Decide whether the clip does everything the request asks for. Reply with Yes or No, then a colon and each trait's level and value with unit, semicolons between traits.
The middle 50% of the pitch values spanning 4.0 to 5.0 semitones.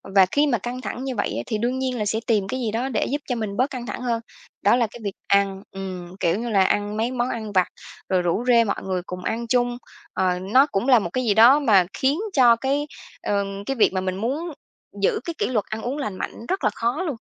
Yes: average, 4.3 semitones